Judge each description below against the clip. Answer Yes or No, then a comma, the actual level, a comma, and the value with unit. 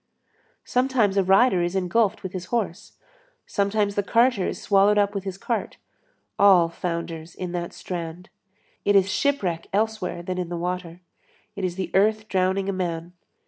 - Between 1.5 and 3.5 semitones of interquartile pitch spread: Yes, average, 2.7 semitones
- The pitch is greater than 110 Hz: Yes, high, 190 Hz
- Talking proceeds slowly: No, average, 165 wpm